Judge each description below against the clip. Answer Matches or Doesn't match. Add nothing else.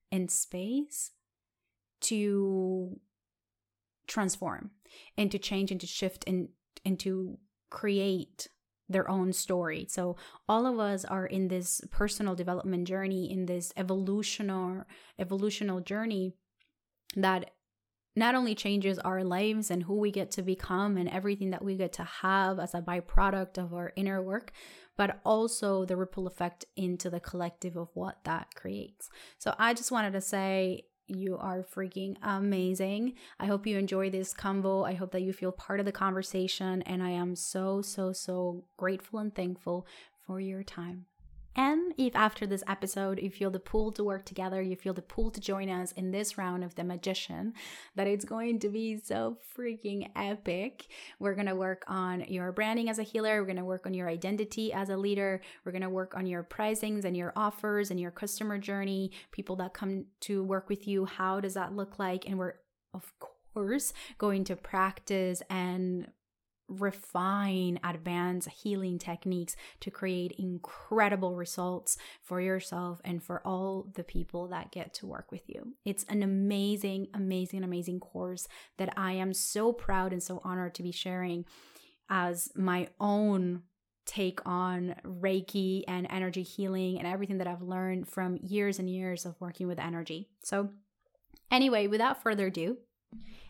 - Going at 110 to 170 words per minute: Matches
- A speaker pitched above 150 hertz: Matches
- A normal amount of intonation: Doesn't match